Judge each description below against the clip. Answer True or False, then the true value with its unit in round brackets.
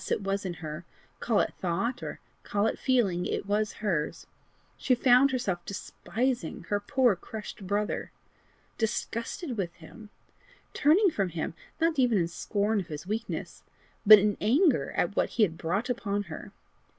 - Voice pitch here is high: True (210 Hz)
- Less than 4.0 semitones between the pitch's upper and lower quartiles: False (4.7 semitones)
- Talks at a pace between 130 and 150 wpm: False (160 wpm)